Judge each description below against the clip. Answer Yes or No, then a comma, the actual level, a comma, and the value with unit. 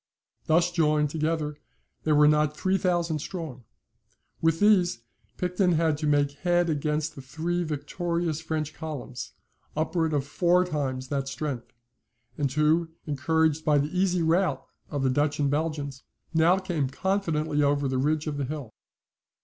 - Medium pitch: Yes, medium, 155 Hz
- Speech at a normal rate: Yes, average, 150 wpm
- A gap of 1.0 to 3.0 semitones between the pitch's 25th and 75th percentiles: Yes, average, 2.7 semitones